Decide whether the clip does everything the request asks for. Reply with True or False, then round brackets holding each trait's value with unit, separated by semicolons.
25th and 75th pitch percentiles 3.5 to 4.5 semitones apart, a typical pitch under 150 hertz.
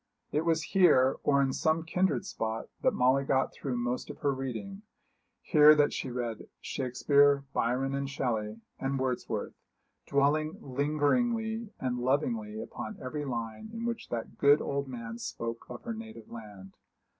True (4.0 semitones; 135 Hz)